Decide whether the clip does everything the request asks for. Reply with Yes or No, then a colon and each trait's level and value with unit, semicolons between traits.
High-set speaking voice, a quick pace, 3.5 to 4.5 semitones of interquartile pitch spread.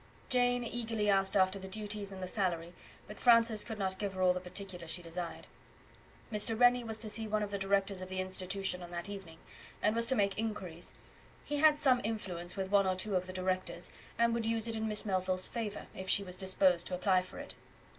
No: high, 195 Hz; fast, 225 wpm; average, 3.0 semitones